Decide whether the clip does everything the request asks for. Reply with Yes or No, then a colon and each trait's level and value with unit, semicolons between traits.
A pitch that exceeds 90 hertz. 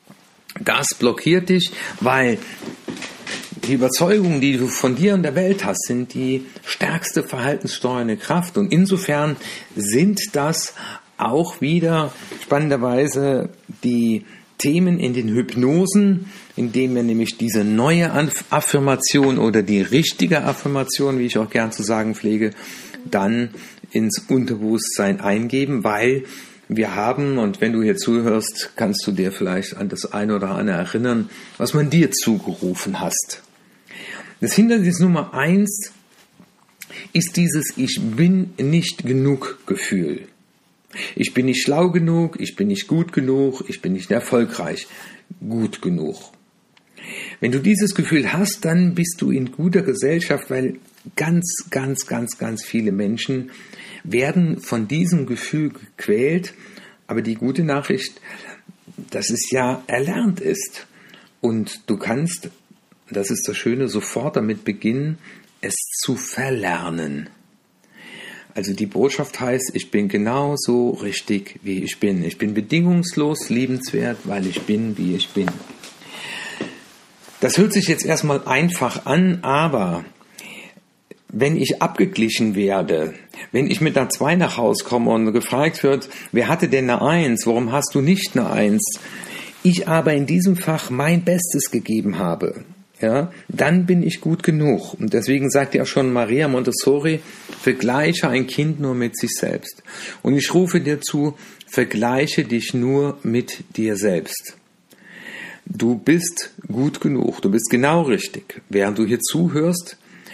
Yes: medium, 140 Hz